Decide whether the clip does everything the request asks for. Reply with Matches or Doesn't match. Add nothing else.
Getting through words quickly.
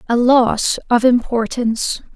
Doesn't match